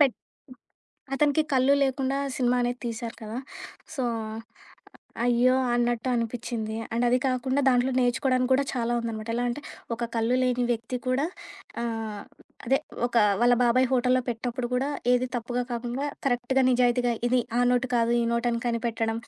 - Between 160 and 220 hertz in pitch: No, high, 245 Hz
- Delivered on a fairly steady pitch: Yes, narrow, 1.4 semitones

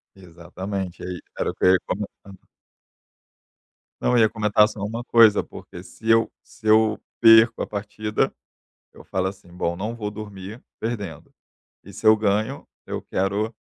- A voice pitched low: Yes, low, 105 Hz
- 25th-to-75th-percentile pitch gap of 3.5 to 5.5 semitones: No, average, 2.7 semitones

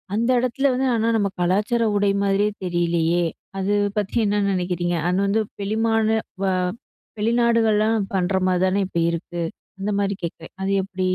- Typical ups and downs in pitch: Yes, average, 3.4 semitones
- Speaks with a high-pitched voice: Yes, high, 200 Hz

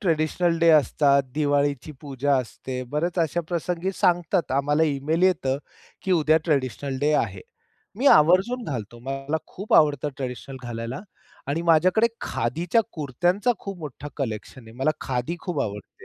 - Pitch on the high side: No, medium, 150 Hz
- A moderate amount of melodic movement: Yes, average, 4.4 semitones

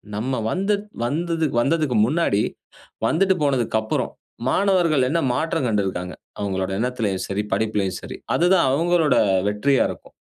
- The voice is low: Yes, low, 130 Hz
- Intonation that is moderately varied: No, wide, 8.0 semitones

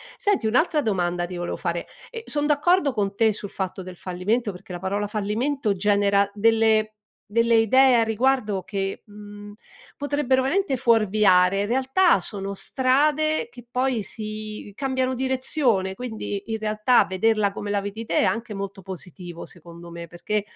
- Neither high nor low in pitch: No, high, 215 Hz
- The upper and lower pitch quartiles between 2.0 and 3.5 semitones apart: No, average, 4.7 semitones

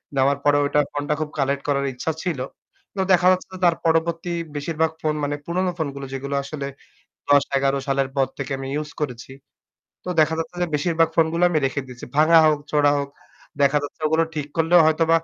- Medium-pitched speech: Yes, medium, 150 Hz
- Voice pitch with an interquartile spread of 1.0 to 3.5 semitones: Yes, average, 2.8 semitones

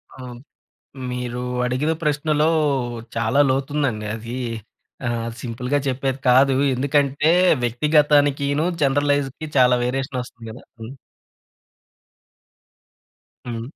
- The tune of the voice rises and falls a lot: No, average, 2.7 semitones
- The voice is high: No, low, 135 Hz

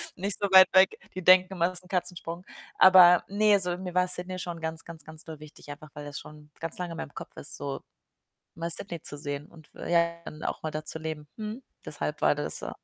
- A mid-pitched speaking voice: Yes, medium, 170 Hz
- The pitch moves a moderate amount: Yes, average, 3.0 semitones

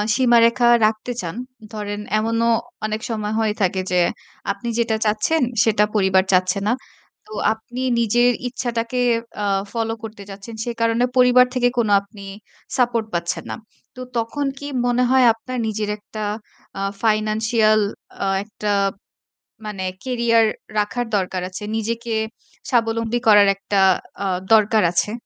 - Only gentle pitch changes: Yes, narrow, 2.3 semitones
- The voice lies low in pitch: No, high, 225 Hz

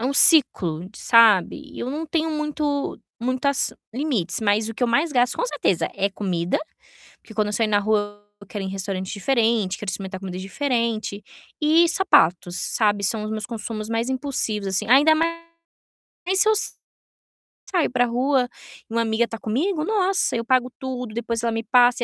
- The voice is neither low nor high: No, high, 230 Hz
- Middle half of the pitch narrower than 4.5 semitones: No, average, 5.1 semitones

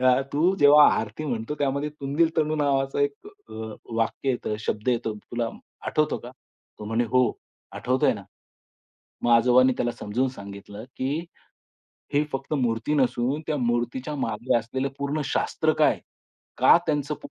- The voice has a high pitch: No, low, 130 Hz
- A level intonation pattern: No, average, 3.7 semitones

